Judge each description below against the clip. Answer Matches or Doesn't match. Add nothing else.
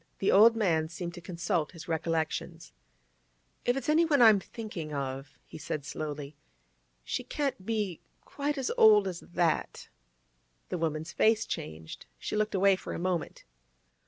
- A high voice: Doesn't match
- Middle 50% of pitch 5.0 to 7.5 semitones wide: Matches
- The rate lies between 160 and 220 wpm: Doesn't match